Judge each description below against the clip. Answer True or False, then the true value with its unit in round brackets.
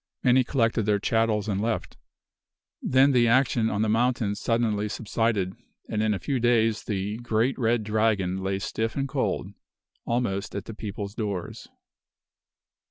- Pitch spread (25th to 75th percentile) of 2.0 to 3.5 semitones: True (2.5 semitones)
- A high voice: False (110 Hz)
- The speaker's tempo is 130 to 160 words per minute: True (150 wpm)